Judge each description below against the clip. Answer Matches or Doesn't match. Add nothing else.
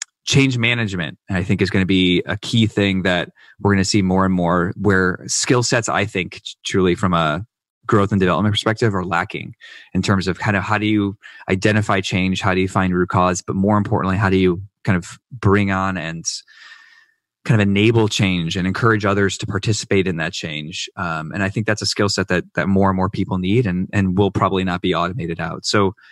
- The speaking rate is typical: Doesn't match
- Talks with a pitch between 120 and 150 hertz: Doesn't match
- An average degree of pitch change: Doesn't match